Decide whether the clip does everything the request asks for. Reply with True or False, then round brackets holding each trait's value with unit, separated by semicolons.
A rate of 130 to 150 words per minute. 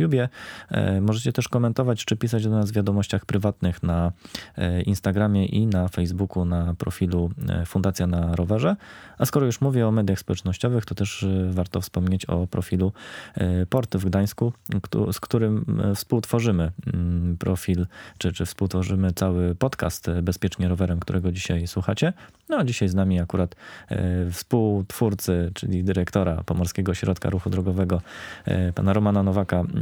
True (135 wpm)